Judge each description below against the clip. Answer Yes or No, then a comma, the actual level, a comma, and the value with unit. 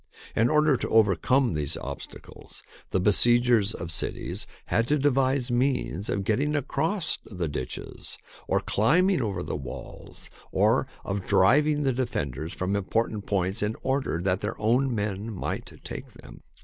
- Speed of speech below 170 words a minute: Yes, average, 150 wpm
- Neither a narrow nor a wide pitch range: No, wide, 5.8 semitones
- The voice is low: Yes, low, 110 Hz